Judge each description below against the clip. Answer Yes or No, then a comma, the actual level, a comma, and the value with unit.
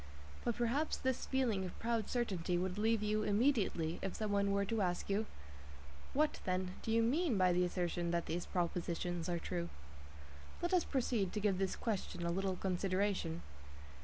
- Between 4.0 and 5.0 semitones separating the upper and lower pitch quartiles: Yes, average, 4.3 semitones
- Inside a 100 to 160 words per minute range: No, average, 175 wpm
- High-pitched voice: Yes, high, 195 Hz